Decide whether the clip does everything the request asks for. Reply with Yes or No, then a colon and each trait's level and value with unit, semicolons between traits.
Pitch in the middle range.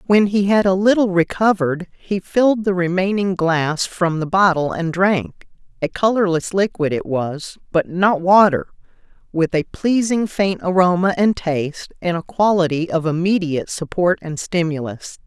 Yes: medium, 180 Hz